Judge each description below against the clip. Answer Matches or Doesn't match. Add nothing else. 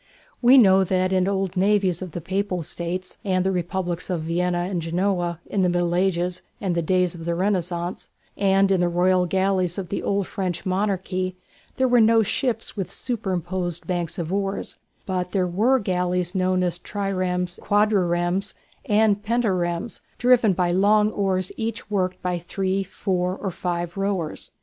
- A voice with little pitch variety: Matches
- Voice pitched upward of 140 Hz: Matches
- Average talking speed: Matches